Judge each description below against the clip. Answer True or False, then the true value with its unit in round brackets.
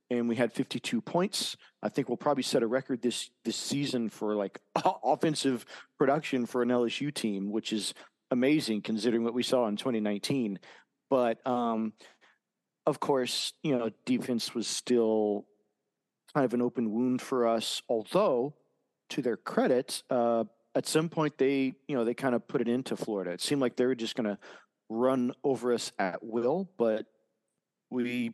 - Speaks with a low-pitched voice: True (120 Hz)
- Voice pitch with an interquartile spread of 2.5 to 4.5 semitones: True (2.9 semitones)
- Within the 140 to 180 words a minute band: True (170 wpm)